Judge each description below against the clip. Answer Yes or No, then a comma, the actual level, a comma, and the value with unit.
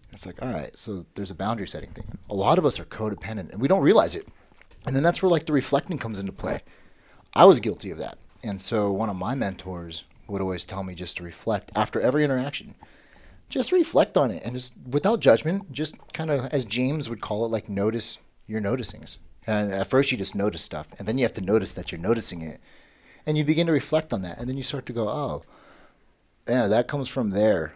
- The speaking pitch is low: Yes, low, 110 Hz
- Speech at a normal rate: No, fast, 235 wpm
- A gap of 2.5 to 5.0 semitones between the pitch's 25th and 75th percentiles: No, wide, 5.6 semitones